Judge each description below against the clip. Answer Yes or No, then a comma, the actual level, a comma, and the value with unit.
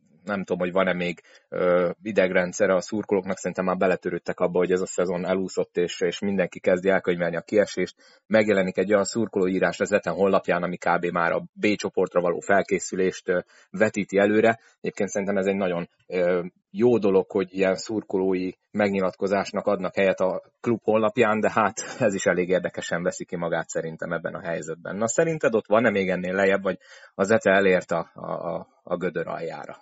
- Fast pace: Yes, fast, 180 wpm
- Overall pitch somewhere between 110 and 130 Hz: No, very low, 95 Hz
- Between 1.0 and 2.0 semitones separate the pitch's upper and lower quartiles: No, average, 2.7 semitones